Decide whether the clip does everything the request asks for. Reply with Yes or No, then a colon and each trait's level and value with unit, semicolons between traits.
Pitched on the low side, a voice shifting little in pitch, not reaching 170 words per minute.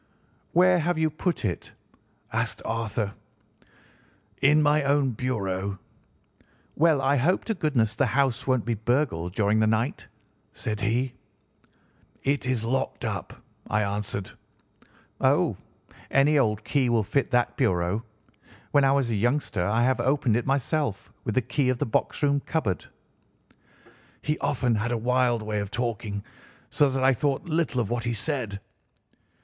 No: low, 120 Hz; average, 4.6 semitones; average, 155 wpm